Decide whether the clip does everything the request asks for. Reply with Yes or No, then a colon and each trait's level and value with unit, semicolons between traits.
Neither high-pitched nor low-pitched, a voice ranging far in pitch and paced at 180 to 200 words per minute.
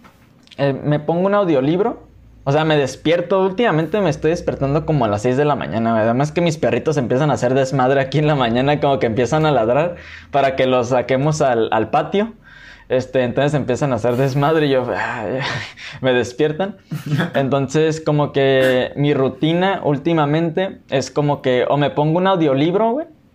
No: medium, 145 Hz; average, 3.3 semitones; average, 185 wpm